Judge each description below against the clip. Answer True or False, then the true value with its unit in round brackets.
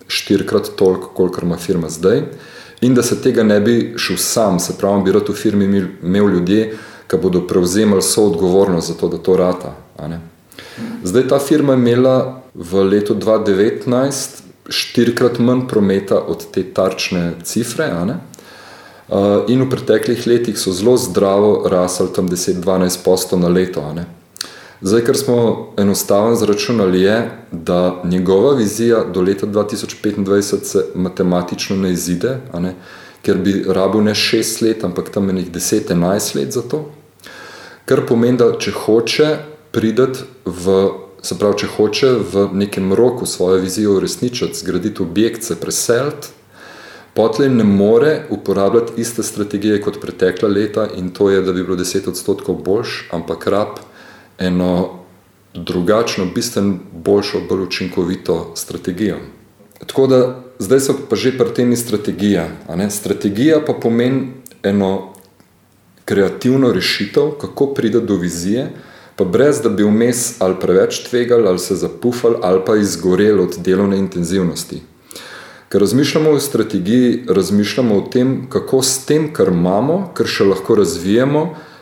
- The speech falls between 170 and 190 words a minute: False (135 wpm)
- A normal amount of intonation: True (4.5 semitones)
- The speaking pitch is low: True (100 Hz)